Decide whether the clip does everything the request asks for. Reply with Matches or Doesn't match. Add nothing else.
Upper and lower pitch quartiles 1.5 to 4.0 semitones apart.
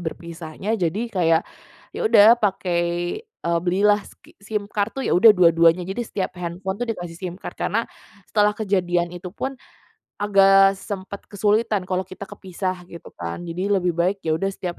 Matches